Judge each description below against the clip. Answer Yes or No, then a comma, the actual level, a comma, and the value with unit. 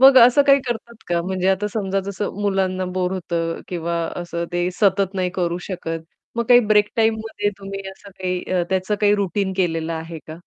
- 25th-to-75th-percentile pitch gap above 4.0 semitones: No, average, 2.9 semitones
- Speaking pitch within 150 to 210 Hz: Yes, high, 190 Hz